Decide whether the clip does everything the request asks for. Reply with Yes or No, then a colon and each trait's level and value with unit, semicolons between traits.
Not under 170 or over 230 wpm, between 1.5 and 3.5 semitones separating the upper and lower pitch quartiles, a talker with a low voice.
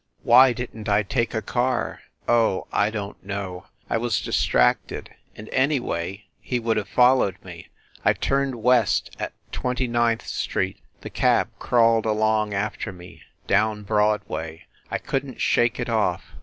No: average, 155 wpm; average, 3.1 semitones; low, 110 Hz